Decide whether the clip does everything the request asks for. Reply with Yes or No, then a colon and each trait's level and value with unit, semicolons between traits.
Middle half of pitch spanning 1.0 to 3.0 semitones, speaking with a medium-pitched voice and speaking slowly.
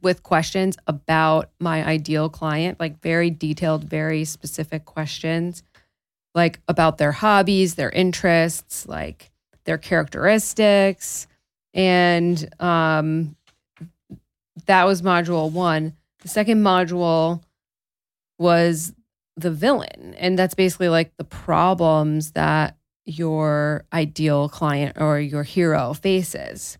Yes: narrow, 2.4 semitones; medium, 165 Hz; slow, 105 wpm